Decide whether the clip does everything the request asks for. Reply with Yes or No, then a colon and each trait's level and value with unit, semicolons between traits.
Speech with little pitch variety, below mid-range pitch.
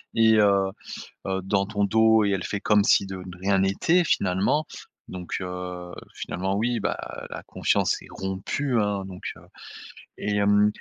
Yes: narrow, 1.8 semitones; low, 100 Hz